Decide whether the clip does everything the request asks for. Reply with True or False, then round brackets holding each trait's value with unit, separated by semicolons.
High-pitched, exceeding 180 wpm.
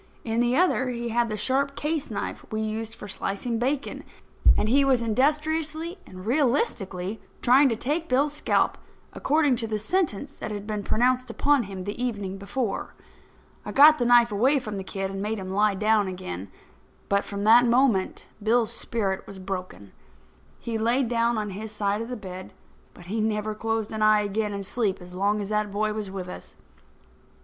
True (220 Hz; 190 wpm)